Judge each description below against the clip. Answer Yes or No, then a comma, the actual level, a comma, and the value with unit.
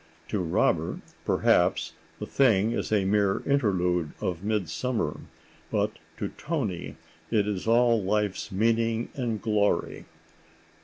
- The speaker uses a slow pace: Yes, slow, 115 wpm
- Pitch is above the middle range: No, low, 105 Hz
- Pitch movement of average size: Yes, average, 3.2 semitones